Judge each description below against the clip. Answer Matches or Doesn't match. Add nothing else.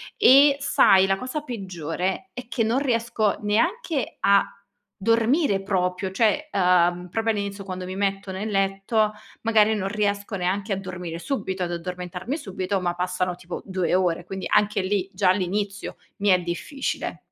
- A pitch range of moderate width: Matches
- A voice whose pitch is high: Matches